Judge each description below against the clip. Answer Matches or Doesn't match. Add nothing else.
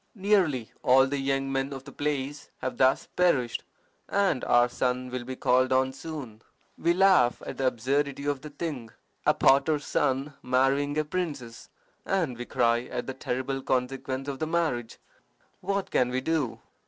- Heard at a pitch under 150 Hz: Matches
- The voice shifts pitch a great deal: Doesn't match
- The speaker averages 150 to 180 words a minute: Matches